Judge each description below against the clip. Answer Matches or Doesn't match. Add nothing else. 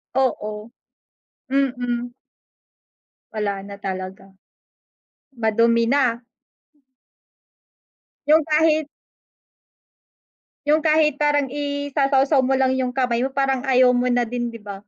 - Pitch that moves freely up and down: Doesn't match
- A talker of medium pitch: Doesn't match